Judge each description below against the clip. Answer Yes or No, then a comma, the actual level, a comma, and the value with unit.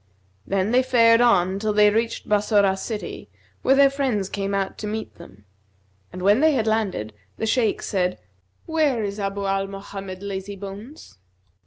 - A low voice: No, high, 205 Hz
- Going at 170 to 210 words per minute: No, average, 155 wpm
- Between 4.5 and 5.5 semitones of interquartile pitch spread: No, average, 2.8 semitones